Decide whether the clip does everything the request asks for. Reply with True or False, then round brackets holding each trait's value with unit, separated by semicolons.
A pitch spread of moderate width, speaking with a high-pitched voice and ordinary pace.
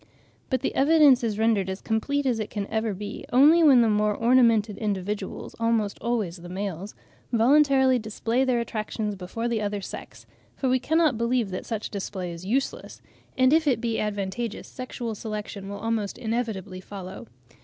True (3.7 semitones; 225 Hz; 170 wpm)